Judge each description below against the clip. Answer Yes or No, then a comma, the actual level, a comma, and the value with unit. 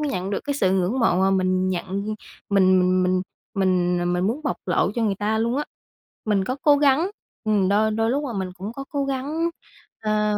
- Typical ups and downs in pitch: No, wide, 5.8 semitones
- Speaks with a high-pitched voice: Yes, high, 210 Hz